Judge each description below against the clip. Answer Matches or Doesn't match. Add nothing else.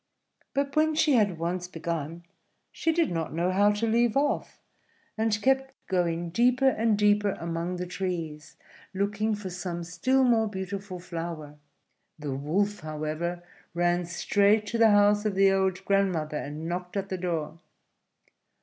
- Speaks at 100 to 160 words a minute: Matches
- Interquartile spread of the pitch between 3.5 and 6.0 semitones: Matches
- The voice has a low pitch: Doesn't match